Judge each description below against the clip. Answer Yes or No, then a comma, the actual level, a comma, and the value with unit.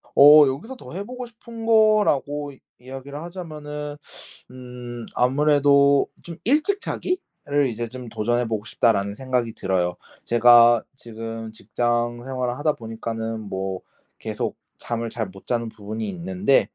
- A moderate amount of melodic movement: Yes, average, 4.7 semitones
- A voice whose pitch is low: Yes, low, 125 Hz